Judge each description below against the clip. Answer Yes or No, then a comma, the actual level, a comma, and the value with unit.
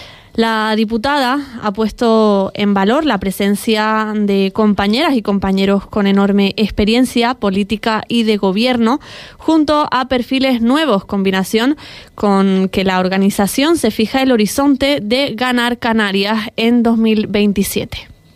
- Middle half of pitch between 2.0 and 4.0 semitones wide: Yes, average, 3.6 semitones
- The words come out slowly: Yes, slow, 120 wpm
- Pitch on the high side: Yes, high, 220 Hz